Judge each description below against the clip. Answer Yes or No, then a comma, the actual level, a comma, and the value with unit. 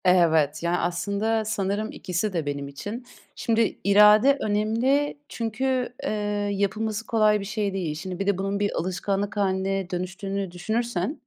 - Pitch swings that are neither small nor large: Yes, average, 3.1 semitones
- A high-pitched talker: Yes, high, 200 Hz